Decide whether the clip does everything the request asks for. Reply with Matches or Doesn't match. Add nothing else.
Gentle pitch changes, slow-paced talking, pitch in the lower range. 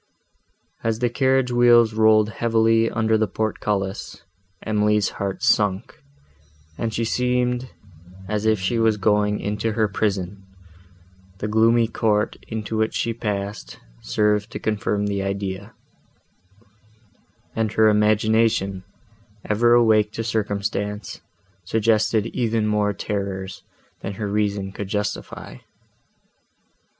Matches